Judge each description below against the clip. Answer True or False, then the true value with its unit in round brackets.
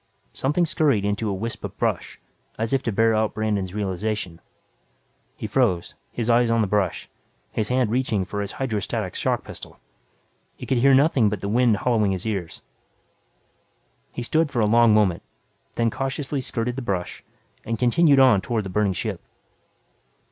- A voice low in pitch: True (110 Hz)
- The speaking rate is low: False (170 wpm)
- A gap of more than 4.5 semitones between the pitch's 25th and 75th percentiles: False (3.5 semitones)